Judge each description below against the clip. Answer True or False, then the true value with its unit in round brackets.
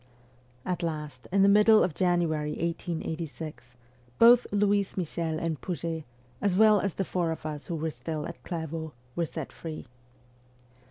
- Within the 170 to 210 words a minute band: False (155 wpm)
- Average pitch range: True (3.3 semitones)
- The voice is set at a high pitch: False (170 Hz)